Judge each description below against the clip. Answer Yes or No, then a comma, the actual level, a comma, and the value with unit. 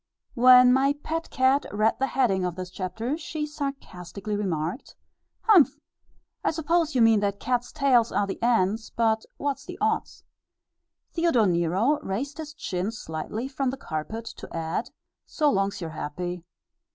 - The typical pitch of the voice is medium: No, high, 230 Hz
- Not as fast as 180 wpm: Yes, average, 150 wpm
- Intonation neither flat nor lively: No, wide, 6.7 semitones